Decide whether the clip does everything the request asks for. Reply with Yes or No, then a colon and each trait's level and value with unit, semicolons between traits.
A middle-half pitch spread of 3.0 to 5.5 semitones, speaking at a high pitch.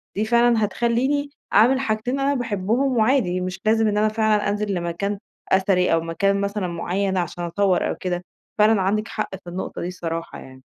Yes: average, 3.5 semitones; high, 205 Hz